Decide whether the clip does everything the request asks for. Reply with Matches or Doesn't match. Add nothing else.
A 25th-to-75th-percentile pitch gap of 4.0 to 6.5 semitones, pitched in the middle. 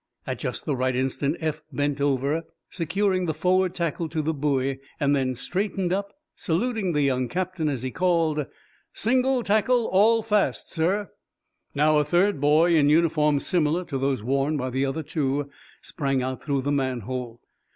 Matches